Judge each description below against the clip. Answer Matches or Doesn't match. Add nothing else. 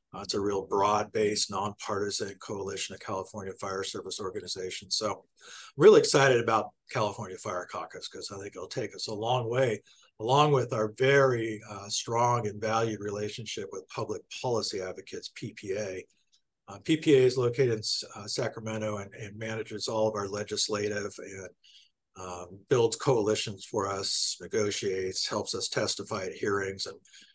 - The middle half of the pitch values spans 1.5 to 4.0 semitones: Matches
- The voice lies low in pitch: Matches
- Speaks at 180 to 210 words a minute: Doesn't match